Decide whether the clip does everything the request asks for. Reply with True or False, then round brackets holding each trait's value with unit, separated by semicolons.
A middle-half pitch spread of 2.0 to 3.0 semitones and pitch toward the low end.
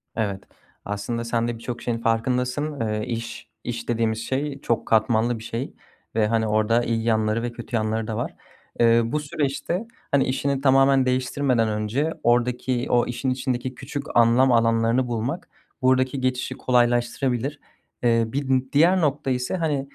True (2.6 semitones; 120 Hz)